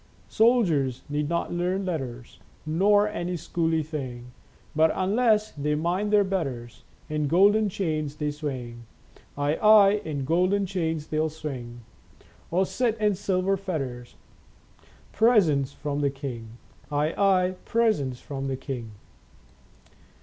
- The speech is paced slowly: Yes, slow, 130 wpm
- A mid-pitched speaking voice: Yes, medium, 160 Hz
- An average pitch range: No, wide, 5.8 semitones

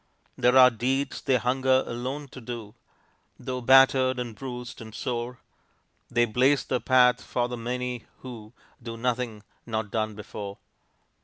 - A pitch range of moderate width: No, narrow, 2.0 semitones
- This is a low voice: Yes, low, 125 Hz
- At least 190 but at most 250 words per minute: No, average, 145 wpm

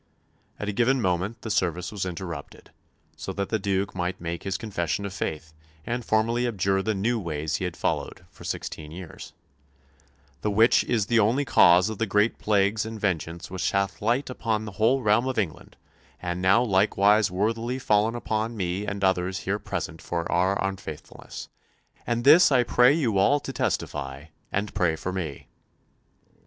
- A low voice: Yes, low, 100 Hz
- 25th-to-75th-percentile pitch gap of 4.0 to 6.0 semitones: No, average, 3.6 semitones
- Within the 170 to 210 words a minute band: Yes, average, 175 wpm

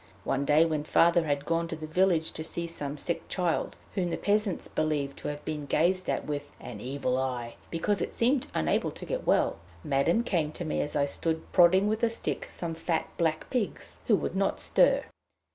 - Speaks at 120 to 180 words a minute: No, fast, 205 wpm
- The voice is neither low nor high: Yes, medium, 160 Hz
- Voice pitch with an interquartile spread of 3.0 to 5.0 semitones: Yes, average, 3.5 semitones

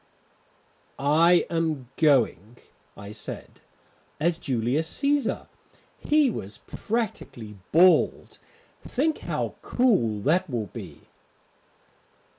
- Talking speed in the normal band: No, slow, 85 wpm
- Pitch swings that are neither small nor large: No, wide, 8.1 semitones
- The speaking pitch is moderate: Yes, medium, 155 Hz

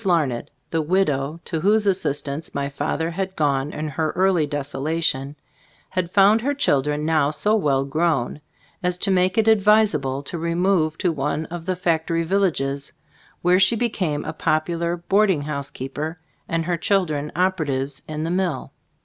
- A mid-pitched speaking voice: Yes, medium, 165 Hz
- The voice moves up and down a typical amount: Yes, average, 4.1 semitones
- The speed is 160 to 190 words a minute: Yes, average, 165 wpm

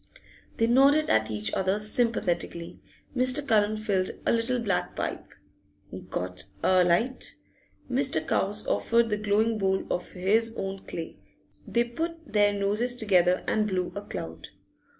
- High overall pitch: Yes, high, 210 Hz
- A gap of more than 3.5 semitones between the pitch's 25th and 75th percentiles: Yes, average, 4.0 semitones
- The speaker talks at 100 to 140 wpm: Yes, slow, 135 wpm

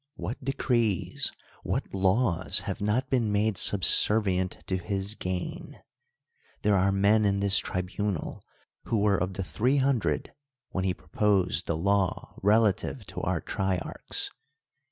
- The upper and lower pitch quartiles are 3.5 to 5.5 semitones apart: No, narrow, 2.6 semitones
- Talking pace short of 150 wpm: Yes, slow, 135 wpm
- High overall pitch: No, low, 100 Hz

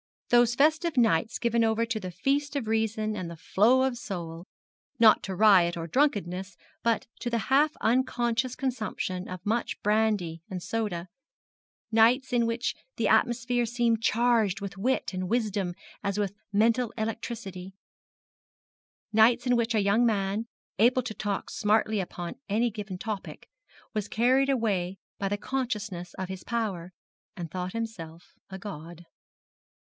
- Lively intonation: No, average, 3.9 semitones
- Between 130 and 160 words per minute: Yes, average, 150 wpm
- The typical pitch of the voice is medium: No, high, 220 Hz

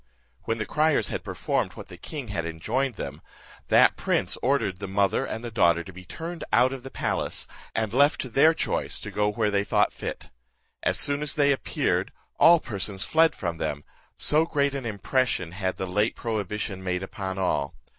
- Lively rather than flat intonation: Yes, wide, 6.4 semitones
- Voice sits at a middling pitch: No, low, 110 Hz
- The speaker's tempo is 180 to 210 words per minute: Yes, average, 195 wpm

